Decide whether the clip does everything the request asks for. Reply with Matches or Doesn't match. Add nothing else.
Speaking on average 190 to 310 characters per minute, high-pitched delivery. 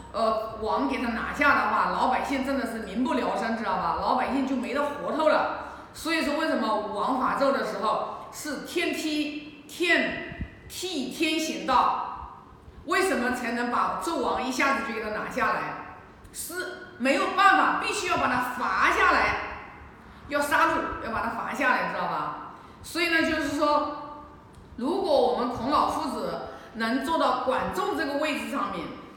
Matches